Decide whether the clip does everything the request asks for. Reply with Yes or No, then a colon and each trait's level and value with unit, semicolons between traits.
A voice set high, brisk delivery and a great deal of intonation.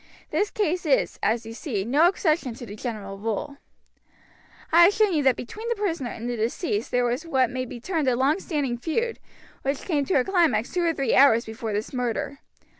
Yes: very high, 265 Hz; fast, 210 wpm; wide, 6.2 semitones